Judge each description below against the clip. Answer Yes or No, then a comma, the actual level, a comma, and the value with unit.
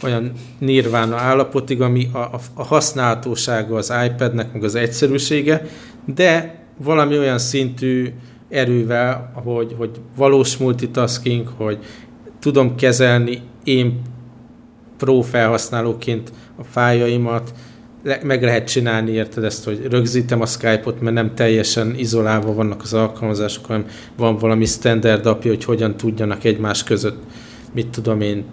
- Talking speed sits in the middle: Yes, average, 125 wpm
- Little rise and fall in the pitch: Yes, narrow, 2.0 semitones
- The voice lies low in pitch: Yes, low, 120 Hz